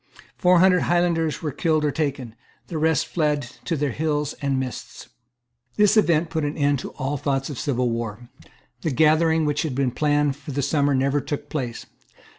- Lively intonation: No, average, 2.9 semitones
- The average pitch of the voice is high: No, medium, 145 Hz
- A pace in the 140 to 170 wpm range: No, average, 185 wpm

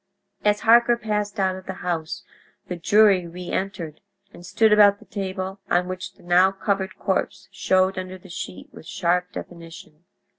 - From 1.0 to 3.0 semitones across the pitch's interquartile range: Yes, narrow, 2.4 semitones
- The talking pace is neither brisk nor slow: Yes, average, 160 wpm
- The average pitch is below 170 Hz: No, medium, 185 Hz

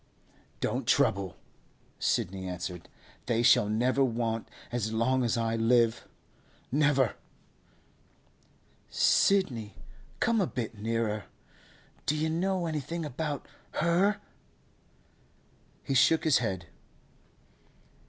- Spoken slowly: Yes, slow, 95 wpm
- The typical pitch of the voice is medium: No, low, 120 Hz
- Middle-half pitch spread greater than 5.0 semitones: Yes, wide, 5.6 semitones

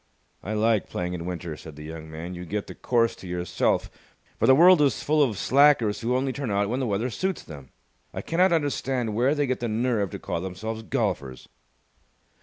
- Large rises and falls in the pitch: Yes, wide, 6.8 semitones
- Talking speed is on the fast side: Yes, fast, 210 wpm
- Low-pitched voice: Yes, low, 110 Hz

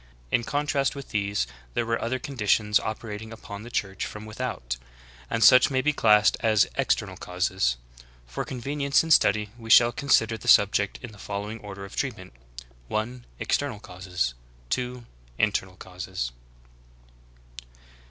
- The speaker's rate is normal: Yes, average, 150 wpm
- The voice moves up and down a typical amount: Yes, average, 3.7 semitones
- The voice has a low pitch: Yes, low, 110 Hz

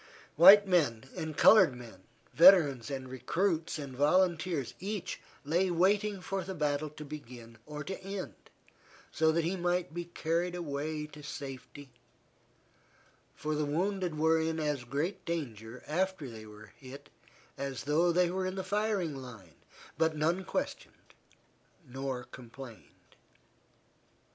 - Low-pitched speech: No, medium, 155 Hz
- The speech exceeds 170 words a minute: No, slow, 135 wpm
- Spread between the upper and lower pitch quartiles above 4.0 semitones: Yes, average, 4.9 semitones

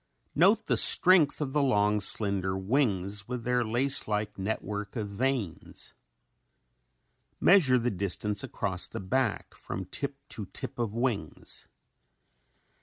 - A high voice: No, low, 110 Hz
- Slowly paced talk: Yes, slow, 125 wpm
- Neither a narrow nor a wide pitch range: Yes, average, 4.7 semitones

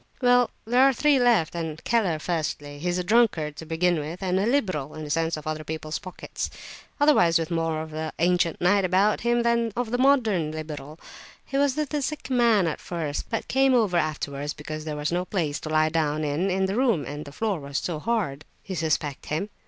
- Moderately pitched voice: Yes, medium, 175 Hz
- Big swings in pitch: Yes, wide, 6.6 semitones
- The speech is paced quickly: Yes, fast, 215 wpm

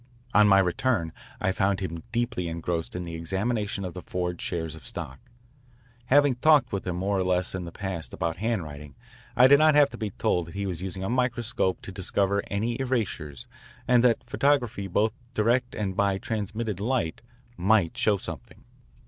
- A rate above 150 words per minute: Yes, average, 180 wpm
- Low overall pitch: Yes, low, 100 Hz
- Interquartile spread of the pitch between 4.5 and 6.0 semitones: Yes, average, 5.0 semitones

